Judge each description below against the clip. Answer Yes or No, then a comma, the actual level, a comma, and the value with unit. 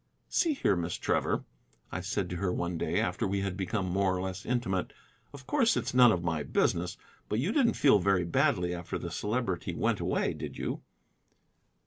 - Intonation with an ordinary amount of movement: Yes, average, 4.9 semitones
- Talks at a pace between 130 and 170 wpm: No, average, 190 wpm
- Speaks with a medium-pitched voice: No, very low, 95 Hz